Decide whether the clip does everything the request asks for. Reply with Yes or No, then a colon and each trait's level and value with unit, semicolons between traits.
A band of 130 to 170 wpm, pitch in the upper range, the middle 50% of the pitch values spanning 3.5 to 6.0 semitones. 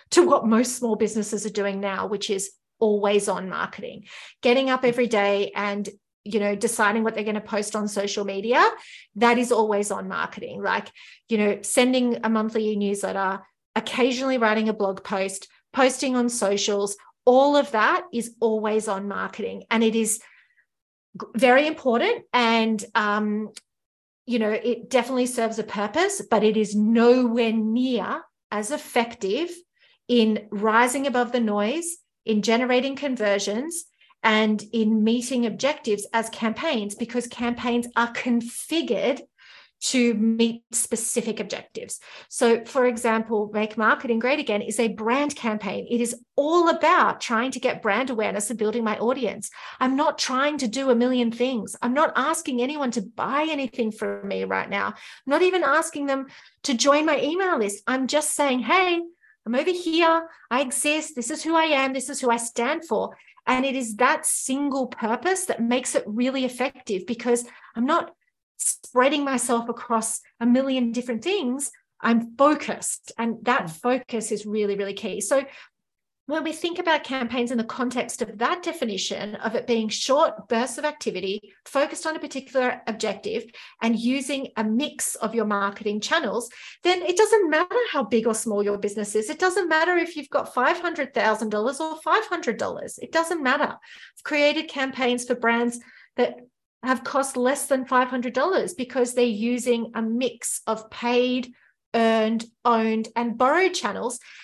Yes: average, 160 wpm; high, 240 Hz; average, 3.9 semitones